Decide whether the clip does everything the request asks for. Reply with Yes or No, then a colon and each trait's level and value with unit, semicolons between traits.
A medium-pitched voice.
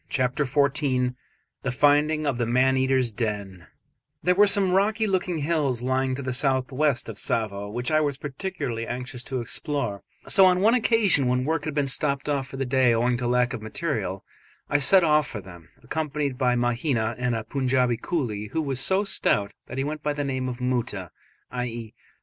No: low, 130 Hz